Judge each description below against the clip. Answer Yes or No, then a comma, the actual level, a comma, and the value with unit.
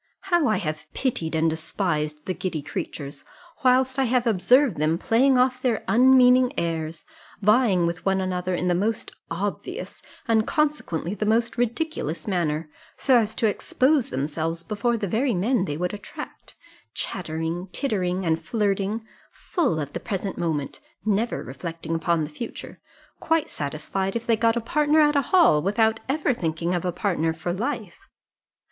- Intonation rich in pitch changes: Yes, wide, 6.8 semitones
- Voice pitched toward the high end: Yes, high, 195 Hz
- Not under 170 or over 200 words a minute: No, average, 160 wpm